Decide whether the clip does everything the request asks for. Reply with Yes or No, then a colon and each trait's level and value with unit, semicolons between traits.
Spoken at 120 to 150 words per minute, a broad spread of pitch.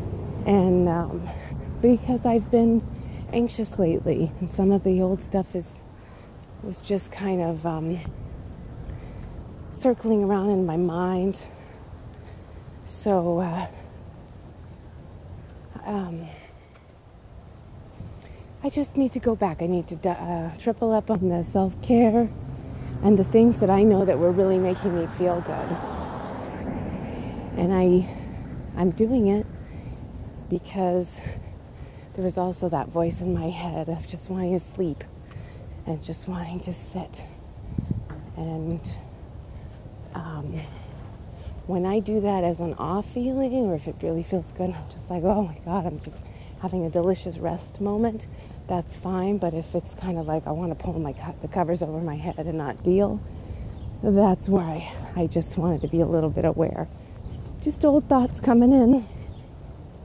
Yes: average, 145 wpm; wide, 7.6 semitones